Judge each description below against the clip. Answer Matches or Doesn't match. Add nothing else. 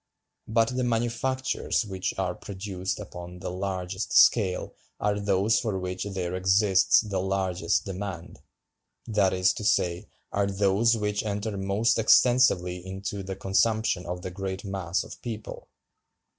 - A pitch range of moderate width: Doesn't match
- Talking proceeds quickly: Doesn't match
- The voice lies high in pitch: Doesn't match